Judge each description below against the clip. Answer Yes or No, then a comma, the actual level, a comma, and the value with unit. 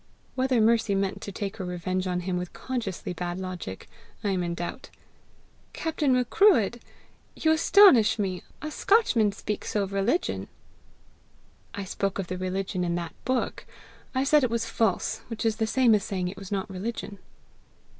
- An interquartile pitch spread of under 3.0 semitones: No, average, 4.4 semitones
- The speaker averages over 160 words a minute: Yes, average, 170 wpm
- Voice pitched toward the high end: Yes, high, 200 Hz